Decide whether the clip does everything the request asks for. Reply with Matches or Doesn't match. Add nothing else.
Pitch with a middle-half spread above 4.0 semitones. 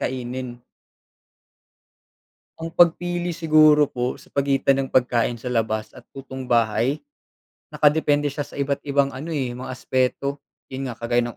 Doesn't match